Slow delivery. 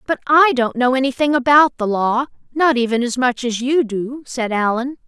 No: average, 200 wpm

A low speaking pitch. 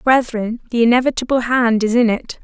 No: high, 240 Hz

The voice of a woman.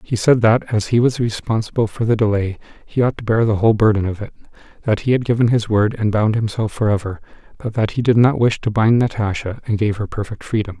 No: male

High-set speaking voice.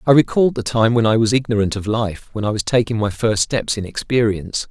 No: low, 110 Hz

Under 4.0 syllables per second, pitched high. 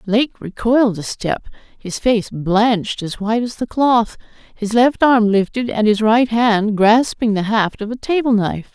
No: 4.4 syllables/s; high, 220 Hz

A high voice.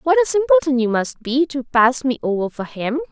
Yes: very high, 270 Hz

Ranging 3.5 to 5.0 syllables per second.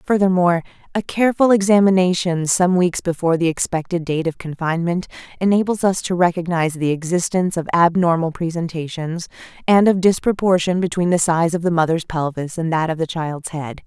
No: 5.7 syllables/s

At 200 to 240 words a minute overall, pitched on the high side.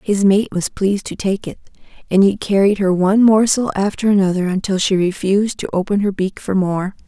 Yes: fast, 205 wpm; high, 195 Hz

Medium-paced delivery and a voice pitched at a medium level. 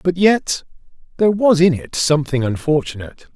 Yes: average, 145 wpm; medium, 155 Hz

